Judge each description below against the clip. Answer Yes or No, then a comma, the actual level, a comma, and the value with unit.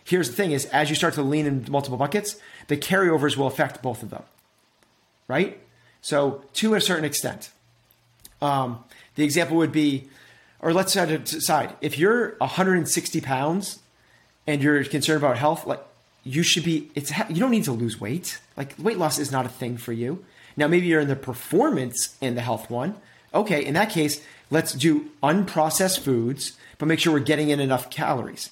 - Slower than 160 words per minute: No, average, 185 wpm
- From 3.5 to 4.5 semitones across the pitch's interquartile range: Yes, average, 4.0 semitones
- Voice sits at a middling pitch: Yes, medium, 150 Hz